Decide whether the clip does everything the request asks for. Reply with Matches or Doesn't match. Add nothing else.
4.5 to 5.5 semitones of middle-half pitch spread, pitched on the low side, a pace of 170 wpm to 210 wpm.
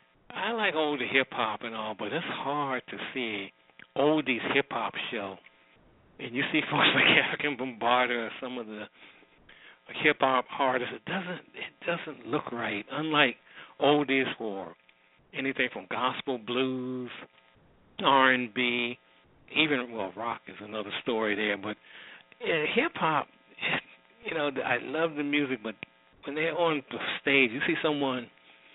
Doesn't match